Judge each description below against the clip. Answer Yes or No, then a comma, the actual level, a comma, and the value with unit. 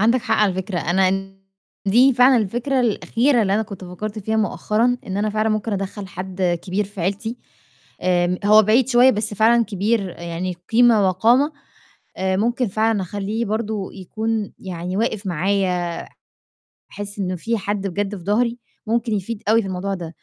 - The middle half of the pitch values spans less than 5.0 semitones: Yes, average, 3.1 semitones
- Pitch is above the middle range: Yes, high, 205 Hz